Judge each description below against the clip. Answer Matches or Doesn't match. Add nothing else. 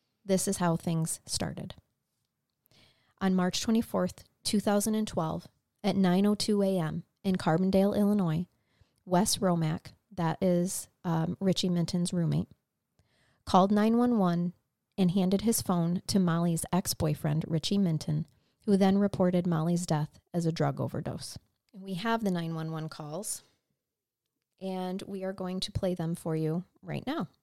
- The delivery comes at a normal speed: Doesn't match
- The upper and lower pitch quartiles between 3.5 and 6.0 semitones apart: Doesn't match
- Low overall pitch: Doesn't match